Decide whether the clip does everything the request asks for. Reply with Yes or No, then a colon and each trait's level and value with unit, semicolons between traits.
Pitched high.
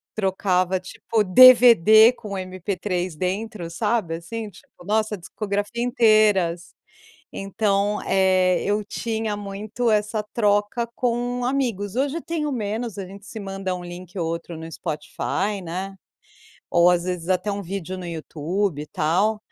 Yes: high, 200 Hz